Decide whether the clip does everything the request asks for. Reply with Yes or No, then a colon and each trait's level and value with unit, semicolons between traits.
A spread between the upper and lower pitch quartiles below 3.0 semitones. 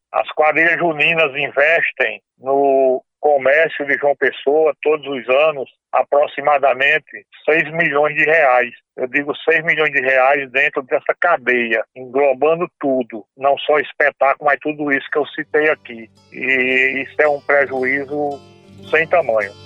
Yes: narrow, 2.6 semitones